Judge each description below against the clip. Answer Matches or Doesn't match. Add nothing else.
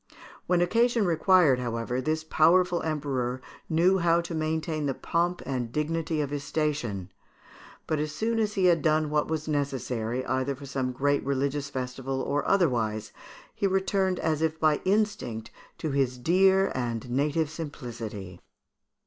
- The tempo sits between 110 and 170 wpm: Matches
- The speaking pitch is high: Doesn't match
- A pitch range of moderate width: Matches